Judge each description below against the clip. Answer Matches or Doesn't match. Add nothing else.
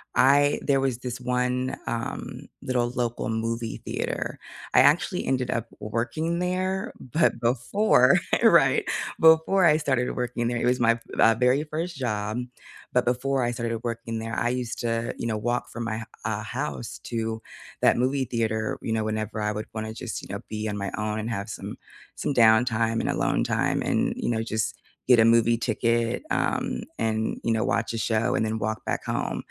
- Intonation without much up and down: Matches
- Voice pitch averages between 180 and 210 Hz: Doesn't match